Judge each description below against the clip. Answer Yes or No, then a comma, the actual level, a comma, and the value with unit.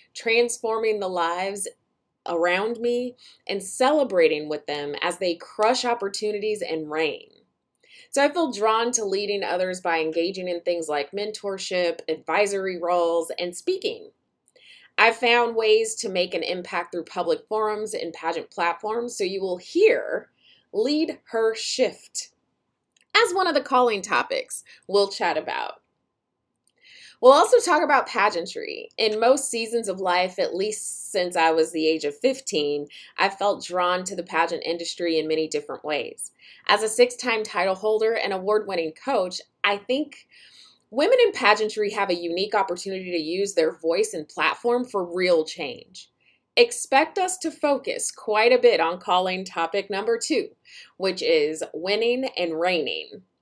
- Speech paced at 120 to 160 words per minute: Yes, average, 150 wpm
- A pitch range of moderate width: No, wide, 7.4 semitones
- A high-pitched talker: Yes, high, 215 Hz